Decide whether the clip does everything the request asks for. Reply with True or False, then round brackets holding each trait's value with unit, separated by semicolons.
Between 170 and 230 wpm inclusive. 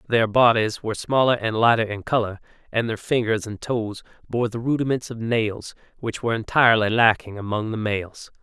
True (180 wpm)